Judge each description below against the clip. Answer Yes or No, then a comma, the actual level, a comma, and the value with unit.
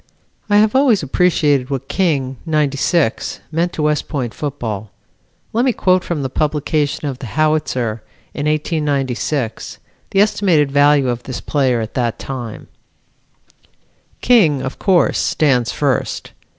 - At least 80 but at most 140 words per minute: Yes, slow, 135 wpm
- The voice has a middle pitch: Yes, medium, 145 Hz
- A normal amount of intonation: Yes, average, 3.8 semitones